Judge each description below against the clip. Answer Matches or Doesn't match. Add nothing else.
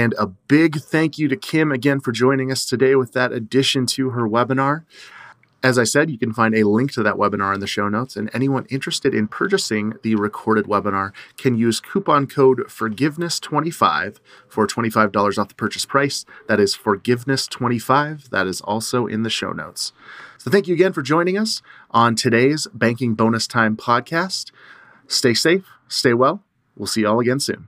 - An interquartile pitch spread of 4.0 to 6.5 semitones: Matches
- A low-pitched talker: Matches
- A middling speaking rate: Matches